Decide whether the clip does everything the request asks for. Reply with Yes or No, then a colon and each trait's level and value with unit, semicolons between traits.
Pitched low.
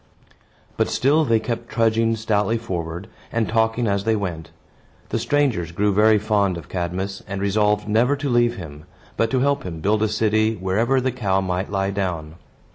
Yes: low, 105 Hz